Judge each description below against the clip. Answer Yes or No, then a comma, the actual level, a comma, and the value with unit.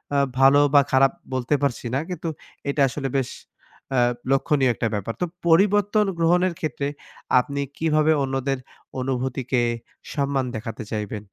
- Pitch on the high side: No, low, 135 Hz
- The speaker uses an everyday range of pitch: Yes, average, 3.4 semitones